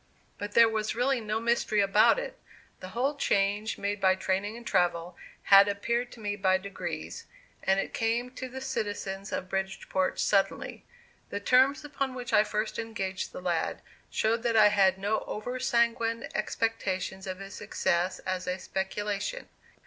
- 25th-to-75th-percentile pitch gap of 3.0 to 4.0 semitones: Yes, average, 3.5 semitones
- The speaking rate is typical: Yes, average, 165 wpm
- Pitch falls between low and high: No, high, 210 Hz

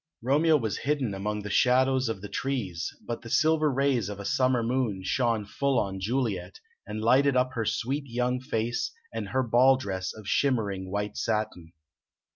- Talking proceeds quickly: No, average, 175 wpm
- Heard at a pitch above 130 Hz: No, low, 120 Hz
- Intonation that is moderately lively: Yes, average, 4.2 semitones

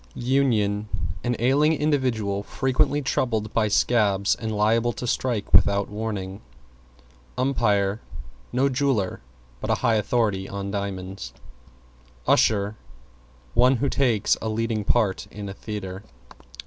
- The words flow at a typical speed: No, slow, 120 wpm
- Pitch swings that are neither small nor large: Yes, average, 3.7 semitones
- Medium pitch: No, low, 110 Hz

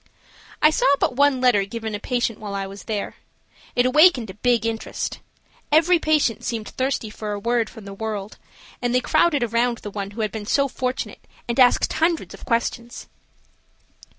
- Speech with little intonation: No, average, 3.4 semitones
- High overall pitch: Yes, high, 235 Hz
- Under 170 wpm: No, average, 180 wpm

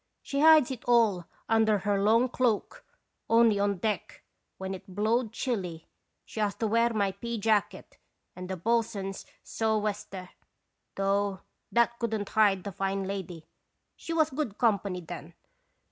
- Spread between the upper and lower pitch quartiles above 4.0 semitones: No, average, 3.0 semitones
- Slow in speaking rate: No, average, 145 wpm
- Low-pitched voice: No, high, 210 Hz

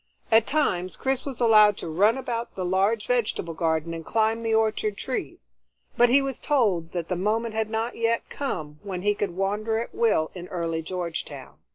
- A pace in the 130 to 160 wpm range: No, average, 190 wpm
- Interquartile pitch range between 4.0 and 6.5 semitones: Yes, average, 4.7 semitones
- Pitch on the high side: Yes, high, 210 Hz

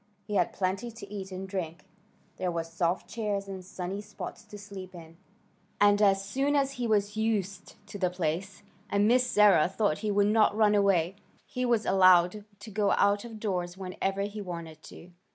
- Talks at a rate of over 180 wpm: Yes, average, 190 wpm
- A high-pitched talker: Yes, high, 200 Hz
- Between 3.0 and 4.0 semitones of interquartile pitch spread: No, narrow, 2.5 semitones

